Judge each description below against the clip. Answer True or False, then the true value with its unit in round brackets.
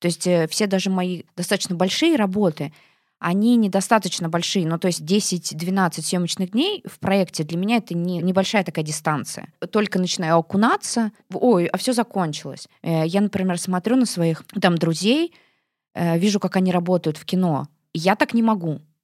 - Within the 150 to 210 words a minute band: True (160 wpm)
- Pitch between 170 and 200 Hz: True (185 Hz)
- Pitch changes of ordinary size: True (3.4 semitones)